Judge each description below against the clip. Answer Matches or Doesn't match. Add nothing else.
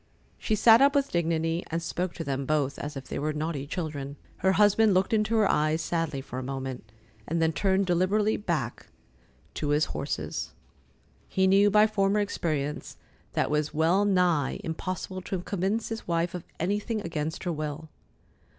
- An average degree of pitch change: Matches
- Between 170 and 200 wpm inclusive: Matches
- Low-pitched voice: Doesn't match